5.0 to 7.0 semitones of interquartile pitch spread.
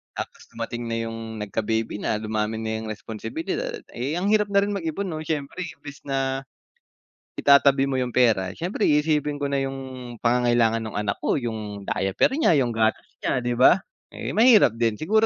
Yes: wide, 5.5 semitones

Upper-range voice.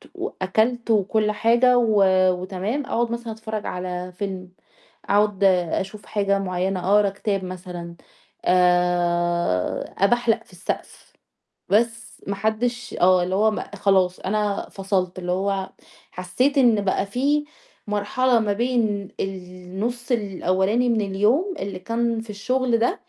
Yes: high, 200 Hz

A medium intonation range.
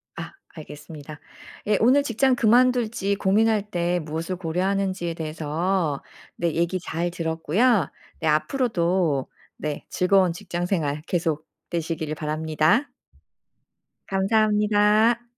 Yes: average, 4.7 semitones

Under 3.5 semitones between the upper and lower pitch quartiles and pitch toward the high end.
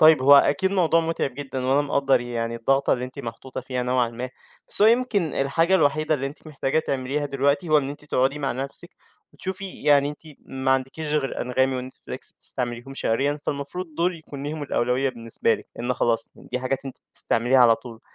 No: average, 2.9 semitones; low, 135 Hz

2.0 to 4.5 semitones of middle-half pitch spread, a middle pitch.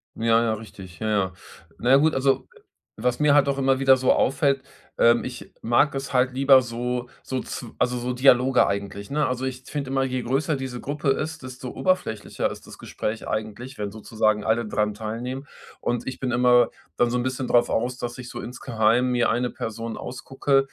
No: narrow, 2.4 semitones; low, 125 Hz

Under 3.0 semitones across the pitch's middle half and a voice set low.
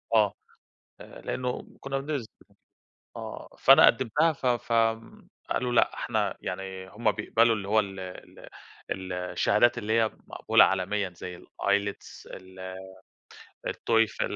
No: average, 3.8 semitones; low, 105 Hz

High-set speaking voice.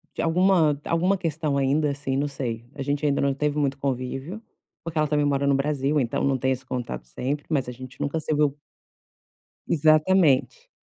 No: medium, 145 Hz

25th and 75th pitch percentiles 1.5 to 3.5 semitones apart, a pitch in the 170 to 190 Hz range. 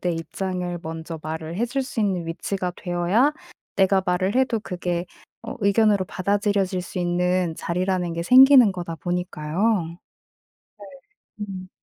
Yes: narrow, 2.6 semitones; medium, 185 Hz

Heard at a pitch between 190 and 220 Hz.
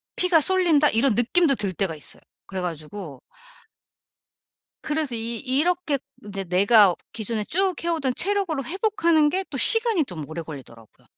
No: very high, 260 Hz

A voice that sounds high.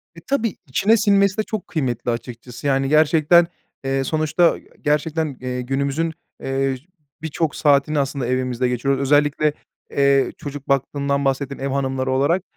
No: medium, 140 Hz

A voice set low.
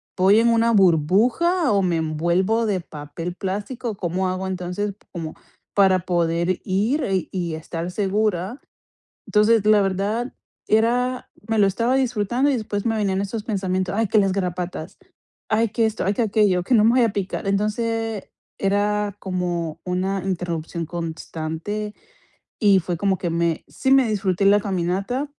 No: high, 195 Hz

